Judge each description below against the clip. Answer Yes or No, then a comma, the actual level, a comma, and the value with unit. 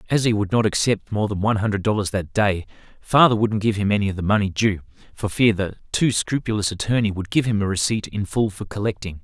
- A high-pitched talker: No, low, 105 Hz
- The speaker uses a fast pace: Yes, fast, 235 wpm